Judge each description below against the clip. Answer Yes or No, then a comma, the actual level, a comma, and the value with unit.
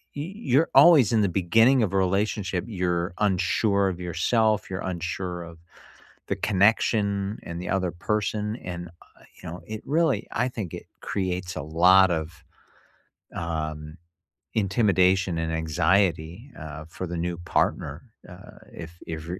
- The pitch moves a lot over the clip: No, average, 3.6 semitones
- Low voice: Yes, very low, 95 Hz